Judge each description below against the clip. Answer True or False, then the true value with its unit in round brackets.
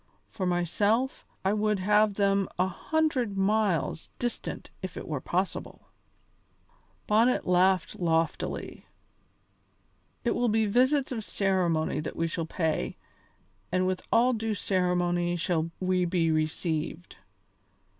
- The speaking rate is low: True (120 wpm)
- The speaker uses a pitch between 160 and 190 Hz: True (185 Hz)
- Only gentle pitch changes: False (3.6 semitones)